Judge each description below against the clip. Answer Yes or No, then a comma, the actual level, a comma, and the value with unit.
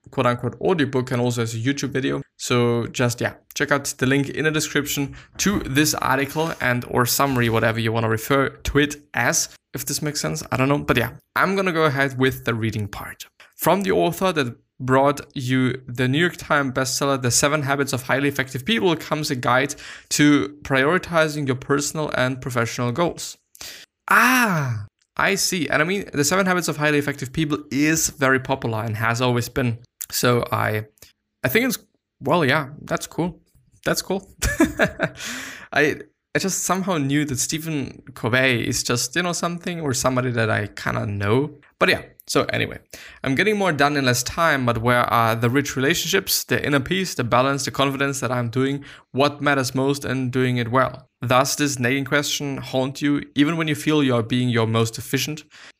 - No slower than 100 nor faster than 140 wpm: No, average, 190 wpm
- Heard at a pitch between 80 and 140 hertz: Yes, low, 135 Hz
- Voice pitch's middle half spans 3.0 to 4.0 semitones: Yes, average, 3.3 semitones